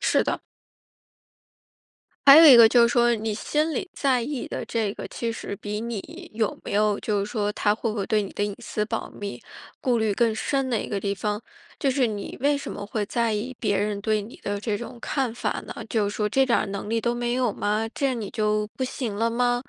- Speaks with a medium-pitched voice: No, high, 225 Hz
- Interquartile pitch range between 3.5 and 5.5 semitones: No, average, 2.7 semitones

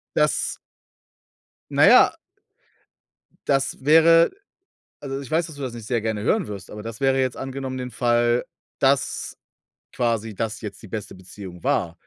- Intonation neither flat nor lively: Yes, average, 4.2 semitones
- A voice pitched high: No, low, 120 Hz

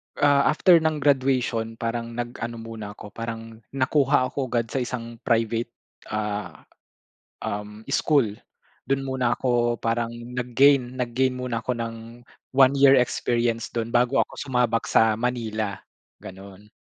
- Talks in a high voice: No, low, 120 Hz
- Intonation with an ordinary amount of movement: No, narrow, 2.2 semitones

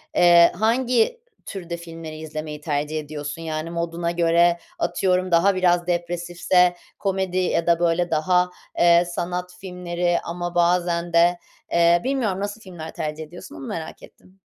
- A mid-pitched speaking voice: Yes, medium, 175 Hz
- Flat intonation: Yes, narrow, 1.4 semitones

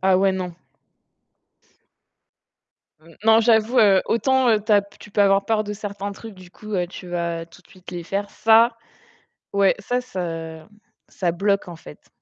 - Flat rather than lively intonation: No, average, 3.2 semitones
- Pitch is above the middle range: Yes, high, 200 Hz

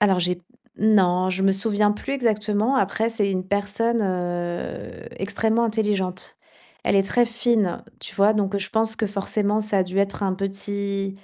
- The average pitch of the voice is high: Yes, high, 200 Hz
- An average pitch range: No, narrow, 2.2 semitones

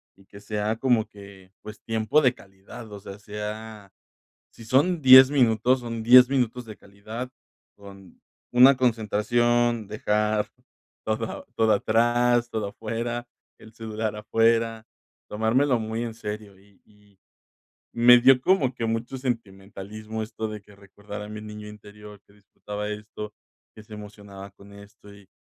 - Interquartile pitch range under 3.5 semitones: Yes, narrow, 2.4 semitones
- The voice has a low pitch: Yes, low, 110 Hz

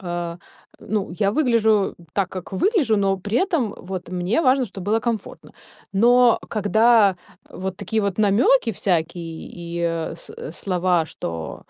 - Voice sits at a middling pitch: No, high, 195 Hz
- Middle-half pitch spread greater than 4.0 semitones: Yes, average, 4.4 semitones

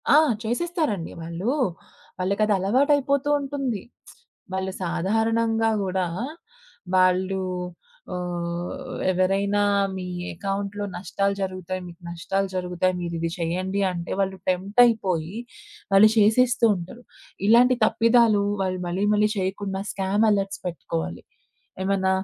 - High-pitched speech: Yes, high, 195 Hz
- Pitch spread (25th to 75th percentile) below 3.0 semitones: No, average, 3.3 semitones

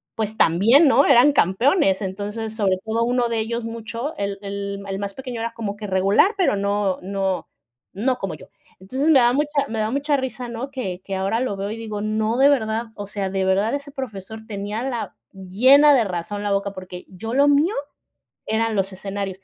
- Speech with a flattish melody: No, average, 4.1 semitones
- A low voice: No, high, 220 Hz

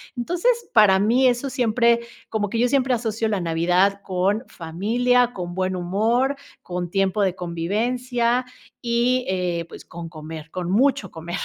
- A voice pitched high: Yes, high, 210 Hz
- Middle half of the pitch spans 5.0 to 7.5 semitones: Yes, wide, 5.4 semitones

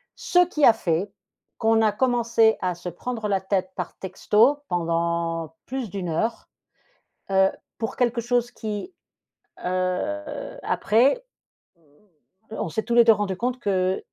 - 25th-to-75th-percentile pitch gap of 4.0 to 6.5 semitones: Yes, average, 4.7 semitones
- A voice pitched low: No, high, 215 Hz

